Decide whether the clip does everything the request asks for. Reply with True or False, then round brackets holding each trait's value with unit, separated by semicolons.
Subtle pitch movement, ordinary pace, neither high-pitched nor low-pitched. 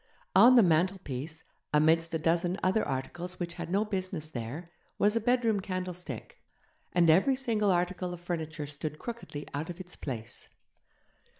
False (3.4 semitones; 155 wpm; 175 Hz)